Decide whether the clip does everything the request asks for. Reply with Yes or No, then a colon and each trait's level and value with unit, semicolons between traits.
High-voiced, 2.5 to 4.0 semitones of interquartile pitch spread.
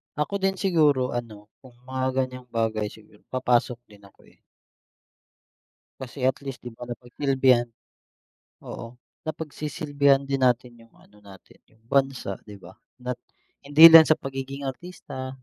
No: low, 130 Hz; average, 2.8 semitones